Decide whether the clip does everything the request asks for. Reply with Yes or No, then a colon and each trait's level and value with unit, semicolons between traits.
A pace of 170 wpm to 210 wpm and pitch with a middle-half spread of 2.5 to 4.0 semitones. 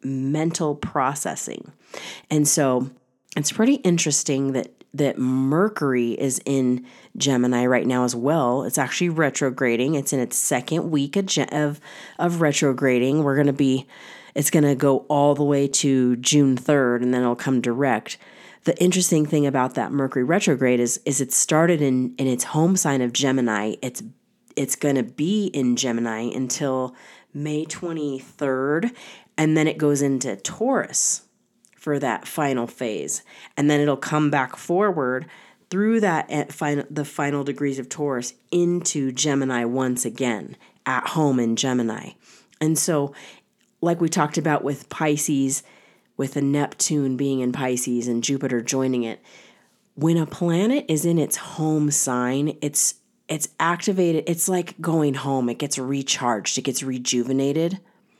No: average, 150 wpm; average, 3.2 semitones